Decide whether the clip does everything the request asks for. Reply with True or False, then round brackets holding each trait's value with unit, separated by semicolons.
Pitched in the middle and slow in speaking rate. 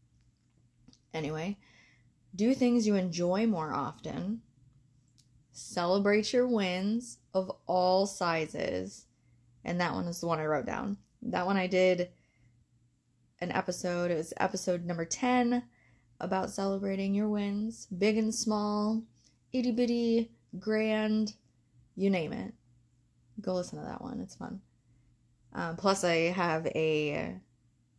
True (180 Hz; 125 wpm)